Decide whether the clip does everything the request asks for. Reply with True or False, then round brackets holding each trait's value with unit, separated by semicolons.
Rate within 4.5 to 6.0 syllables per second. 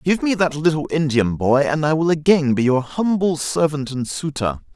True (4.9 syllables/s)